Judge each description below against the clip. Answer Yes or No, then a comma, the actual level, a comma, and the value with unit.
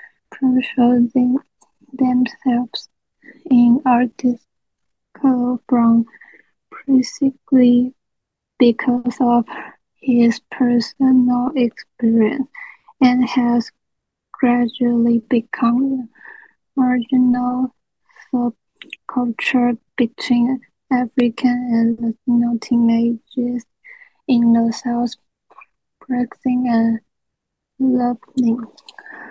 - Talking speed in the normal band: No, slow, 60 wpm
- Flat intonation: Yes, narrow, 1.4 semitones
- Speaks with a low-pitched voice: No, high, 245 Hz